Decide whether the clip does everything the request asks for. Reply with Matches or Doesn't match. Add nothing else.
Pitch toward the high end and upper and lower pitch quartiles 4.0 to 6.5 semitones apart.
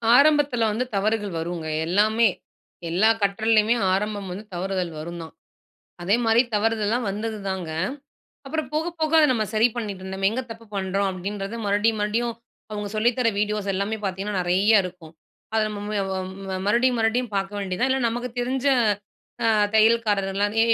Doesn't match